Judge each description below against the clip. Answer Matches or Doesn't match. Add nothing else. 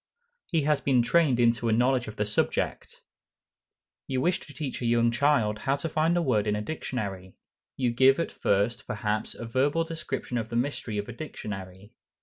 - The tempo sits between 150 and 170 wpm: Doesn't match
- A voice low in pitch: Matches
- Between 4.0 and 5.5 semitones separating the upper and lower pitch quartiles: Matches